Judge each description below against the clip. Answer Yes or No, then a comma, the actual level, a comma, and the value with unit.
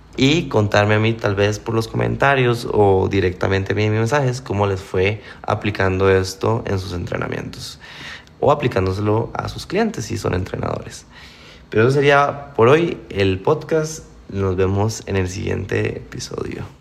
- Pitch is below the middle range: Yes, low, 105 Hz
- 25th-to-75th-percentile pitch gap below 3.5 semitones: No, average, 4.0 semitones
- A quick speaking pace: No, average, 155 wpm